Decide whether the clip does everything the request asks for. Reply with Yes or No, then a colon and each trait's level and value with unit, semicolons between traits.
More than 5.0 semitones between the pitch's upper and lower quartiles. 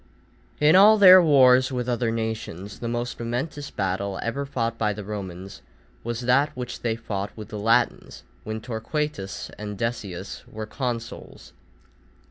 No: average, 3.4 semitones